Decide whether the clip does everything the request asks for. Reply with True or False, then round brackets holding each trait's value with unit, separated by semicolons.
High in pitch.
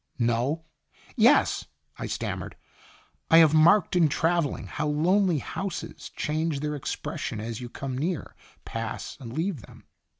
False (155 Hz)